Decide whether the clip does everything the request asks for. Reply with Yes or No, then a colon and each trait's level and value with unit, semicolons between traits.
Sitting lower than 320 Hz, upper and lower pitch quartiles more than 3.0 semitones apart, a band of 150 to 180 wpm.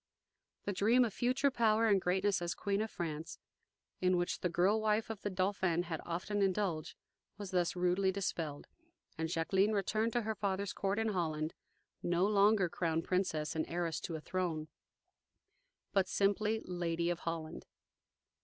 Yes: medium, 185 Hz; average, 3.4 semitones; average, 160 wpm